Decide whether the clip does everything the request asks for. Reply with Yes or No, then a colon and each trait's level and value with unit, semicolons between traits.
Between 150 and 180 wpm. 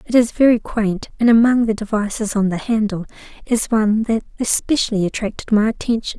Yes: average, 175 wpm